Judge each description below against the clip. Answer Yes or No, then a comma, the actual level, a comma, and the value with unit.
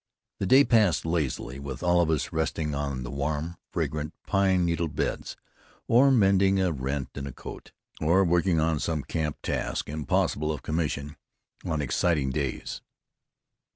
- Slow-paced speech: No, average, 155 wpm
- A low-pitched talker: Yes, very low, 80 Hz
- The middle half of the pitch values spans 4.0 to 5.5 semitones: No, average, 3.5 semitones